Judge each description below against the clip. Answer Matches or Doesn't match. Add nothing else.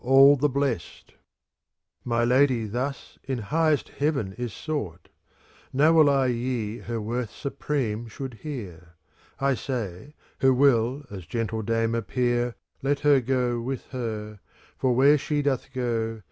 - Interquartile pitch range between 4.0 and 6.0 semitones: Doesn't match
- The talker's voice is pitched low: Matches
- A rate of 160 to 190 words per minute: Doesn't match